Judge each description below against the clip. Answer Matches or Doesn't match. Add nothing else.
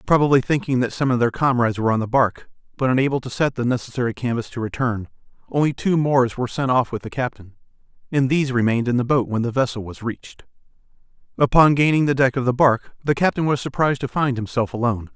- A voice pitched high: Doesn't match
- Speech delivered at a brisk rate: Matches